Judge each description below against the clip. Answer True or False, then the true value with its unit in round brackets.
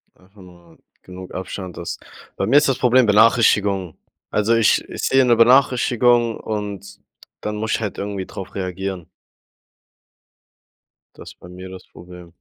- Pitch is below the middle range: True (100 Hz)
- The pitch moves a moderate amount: True (3.8 semitones)